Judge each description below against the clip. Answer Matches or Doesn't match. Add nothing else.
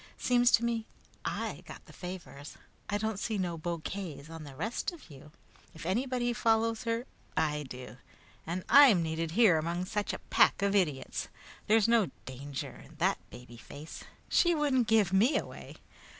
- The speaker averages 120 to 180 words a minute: Matches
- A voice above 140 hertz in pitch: Matches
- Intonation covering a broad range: Matches